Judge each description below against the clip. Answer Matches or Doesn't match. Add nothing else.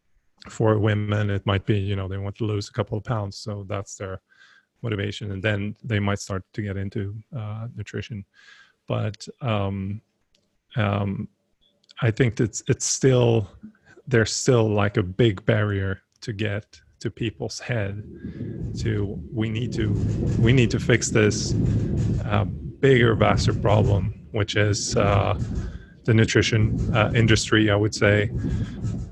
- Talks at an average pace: Matches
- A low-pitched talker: Matches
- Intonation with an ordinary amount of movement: Doesn't match